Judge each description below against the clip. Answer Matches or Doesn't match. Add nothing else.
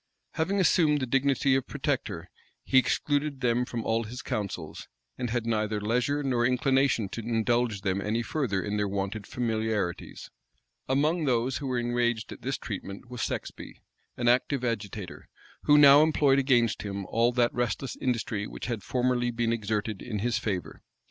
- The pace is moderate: Matches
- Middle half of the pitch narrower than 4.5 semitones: Matches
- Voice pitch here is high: Doesn't match